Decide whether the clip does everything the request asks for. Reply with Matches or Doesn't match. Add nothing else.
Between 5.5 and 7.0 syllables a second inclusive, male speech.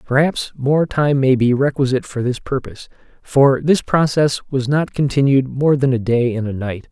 Doesn't match